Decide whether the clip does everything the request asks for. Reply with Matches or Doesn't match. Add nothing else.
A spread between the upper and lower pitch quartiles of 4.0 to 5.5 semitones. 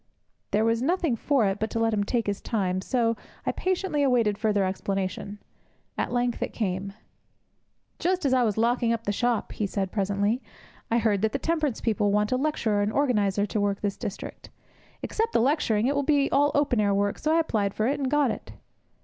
Matches